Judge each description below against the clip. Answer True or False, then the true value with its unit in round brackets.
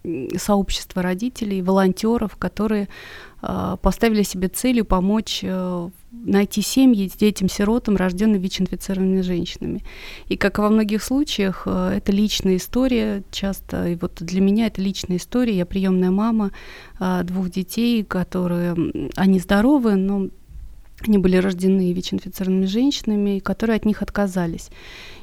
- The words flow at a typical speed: True (130 wpm)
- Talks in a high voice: True (195 Hz)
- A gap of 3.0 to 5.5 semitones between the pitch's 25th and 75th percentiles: False (2.5 semitones)